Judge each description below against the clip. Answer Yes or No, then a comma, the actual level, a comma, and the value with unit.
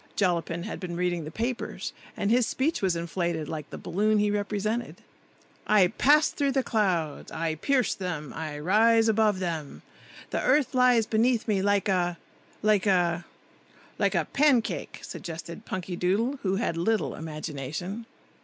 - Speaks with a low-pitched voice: No, high, 195 Hz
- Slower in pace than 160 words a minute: Yes, average, 145 wpm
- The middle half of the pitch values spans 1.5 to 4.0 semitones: No, average, 4.8 semitones